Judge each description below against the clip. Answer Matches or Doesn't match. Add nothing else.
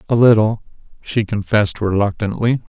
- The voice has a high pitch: Doesn't match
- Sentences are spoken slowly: Matches